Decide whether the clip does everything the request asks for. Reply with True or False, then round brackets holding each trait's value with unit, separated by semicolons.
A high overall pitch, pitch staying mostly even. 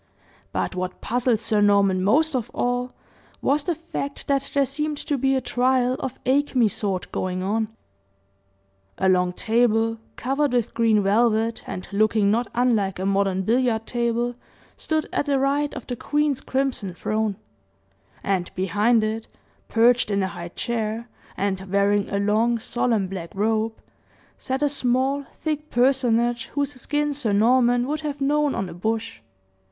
False (235 Hz; 4.6 semitones)